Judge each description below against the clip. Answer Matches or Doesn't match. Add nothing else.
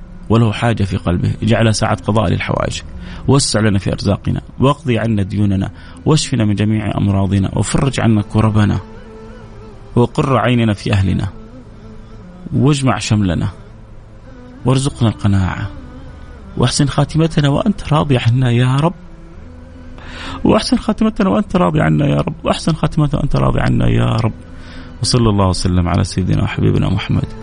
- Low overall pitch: Matches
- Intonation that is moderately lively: Matches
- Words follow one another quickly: Doesn't match